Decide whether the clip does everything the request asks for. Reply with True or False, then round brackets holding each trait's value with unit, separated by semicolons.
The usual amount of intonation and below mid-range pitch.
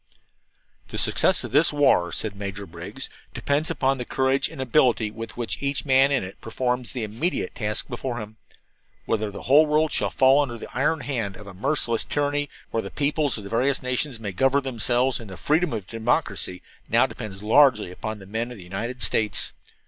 True (4.6 semitones; 120 Hz)